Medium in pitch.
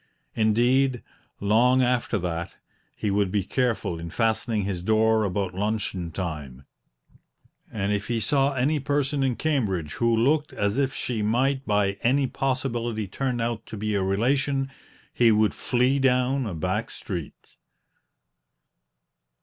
No: low, 115 Hz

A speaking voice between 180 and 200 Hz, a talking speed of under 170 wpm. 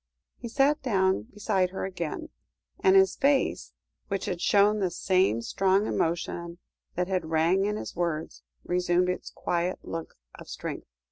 Yes: medium, 185 Hz; average, 150 wpm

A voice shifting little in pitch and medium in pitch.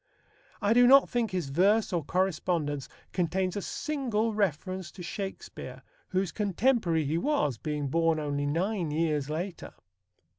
No: average, 5.0 semitones; medium, 180 Hz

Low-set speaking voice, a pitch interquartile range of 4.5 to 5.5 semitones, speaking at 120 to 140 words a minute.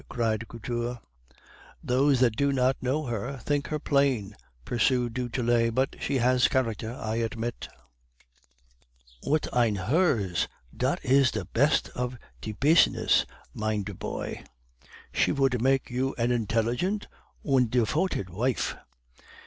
No: low, 125 Hz; average, 3.0 semitones; slow, 135 wpm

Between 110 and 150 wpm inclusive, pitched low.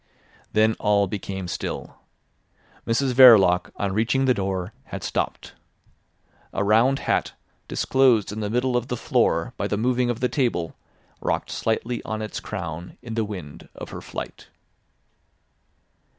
Yes: average, 145 wpm; low, 110 Hz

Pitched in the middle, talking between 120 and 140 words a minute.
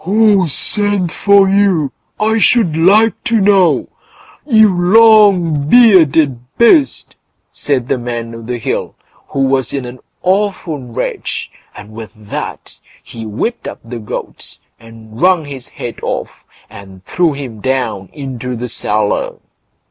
Yes: medium, 145 Hz; slow, 135 wpm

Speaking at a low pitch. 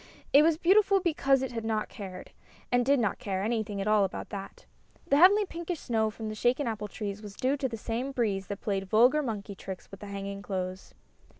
No: high, 220 Hz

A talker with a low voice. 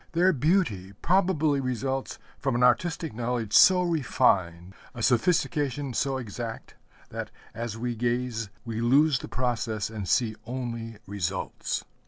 Yes: low, 125 Hz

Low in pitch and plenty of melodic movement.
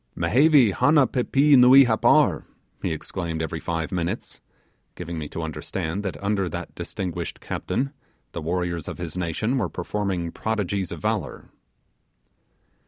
Yes: very low, 95 Hz; wide, 6.5 semitones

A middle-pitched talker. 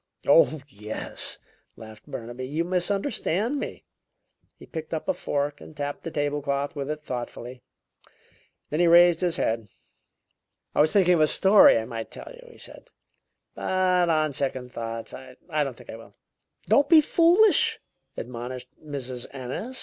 Yes: medium, 145 Hz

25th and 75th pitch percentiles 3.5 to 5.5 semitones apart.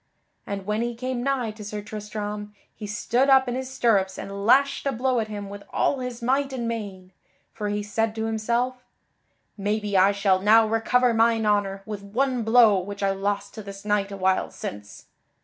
No: average, 3.0 semitones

